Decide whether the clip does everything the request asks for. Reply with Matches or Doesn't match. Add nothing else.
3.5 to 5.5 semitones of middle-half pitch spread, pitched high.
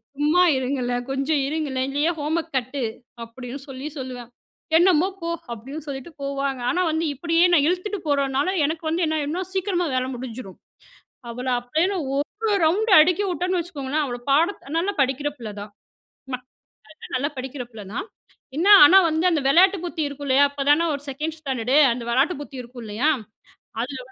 Matches